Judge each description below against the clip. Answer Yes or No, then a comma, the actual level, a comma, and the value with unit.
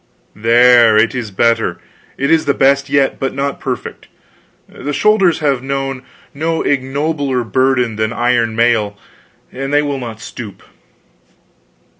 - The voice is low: Yes, low, 130 Hz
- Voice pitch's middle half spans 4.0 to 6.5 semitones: No, average, 3.1 semitones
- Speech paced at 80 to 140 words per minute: Yes, slow, 135 wpm